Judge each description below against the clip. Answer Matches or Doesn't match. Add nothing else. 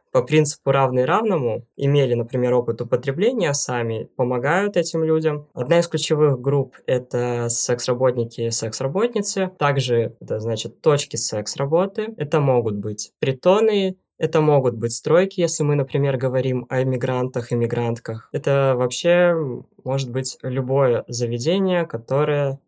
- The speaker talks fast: Doesn't match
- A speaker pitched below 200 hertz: Matches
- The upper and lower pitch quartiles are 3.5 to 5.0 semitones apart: Matches